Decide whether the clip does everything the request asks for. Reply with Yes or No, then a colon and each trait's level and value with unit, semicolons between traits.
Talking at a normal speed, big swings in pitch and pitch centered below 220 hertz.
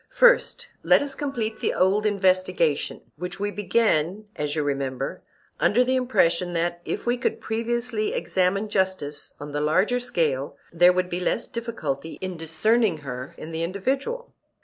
Yes: average, 155 wpm; wide, 6.1 semitones; medium, 185 Hz